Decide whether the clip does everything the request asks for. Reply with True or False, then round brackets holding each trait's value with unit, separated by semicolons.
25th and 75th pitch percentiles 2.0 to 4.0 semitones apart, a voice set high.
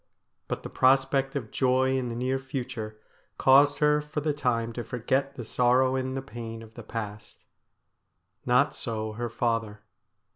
False (2.7 semitones; 125 Hz)